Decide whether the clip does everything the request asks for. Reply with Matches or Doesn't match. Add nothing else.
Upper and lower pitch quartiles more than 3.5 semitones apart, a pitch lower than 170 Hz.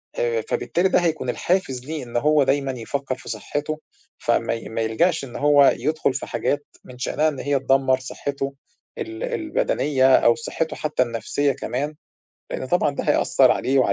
Doesn't match